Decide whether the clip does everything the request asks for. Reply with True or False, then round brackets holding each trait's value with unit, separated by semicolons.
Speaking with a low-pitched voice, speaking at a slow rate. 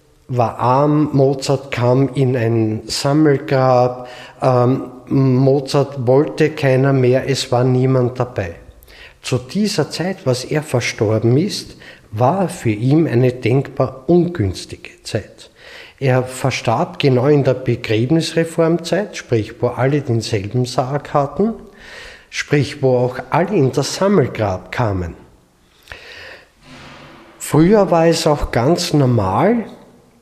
True (130 Hz; 110 wpm)